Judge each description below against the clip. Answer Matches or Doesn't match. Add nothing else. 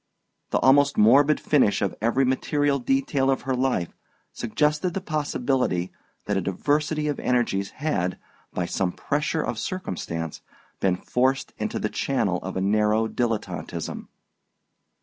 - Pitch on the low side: Matches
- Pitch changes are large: Matches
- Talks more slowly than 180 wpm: Matches